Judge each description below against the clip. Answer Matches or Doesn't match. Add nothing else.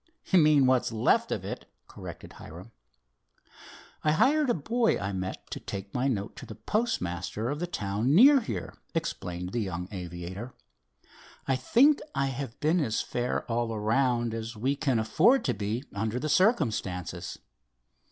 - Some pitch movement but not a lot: Doesn't match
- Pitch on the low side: Matches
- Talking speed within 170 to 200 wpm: Doesn't match